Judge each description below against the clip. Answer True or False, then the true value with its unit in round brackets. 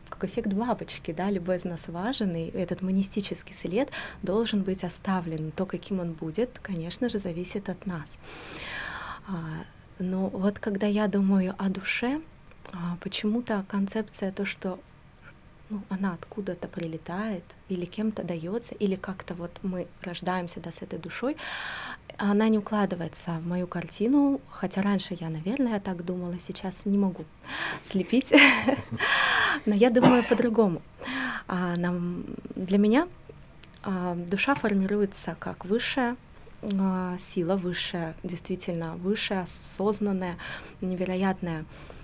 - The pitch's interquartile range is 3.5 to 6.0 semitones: False (3.0 semitones)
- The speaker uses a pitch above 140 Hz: True (190 Hz)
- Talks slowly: False (120 wpm)